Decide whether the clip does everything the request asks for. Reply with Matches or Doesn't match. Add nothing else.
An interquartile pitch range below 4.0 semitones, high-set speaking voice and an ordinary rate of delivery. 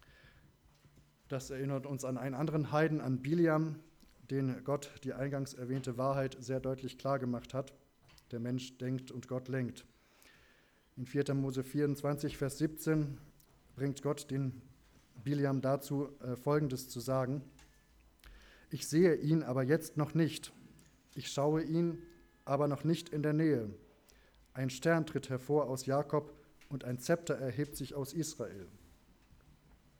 Doesn't match